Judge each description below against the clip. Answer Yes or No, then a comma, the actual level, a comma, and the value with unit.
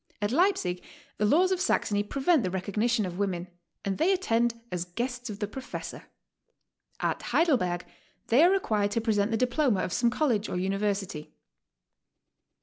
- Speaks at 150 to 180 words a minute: Yes, average, 160 wpm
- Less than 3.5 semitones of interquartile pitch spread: No, average, 5.3 semitones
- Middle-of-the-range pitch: No, high, 220 Hz